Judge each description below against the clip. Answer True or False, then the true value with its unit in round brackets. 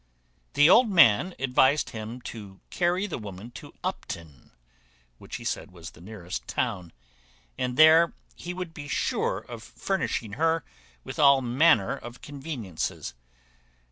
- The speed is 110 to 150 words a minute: True (140 wpm)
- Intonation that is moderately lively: False (7.7 semitones)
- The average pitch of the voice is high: False (125 Hz)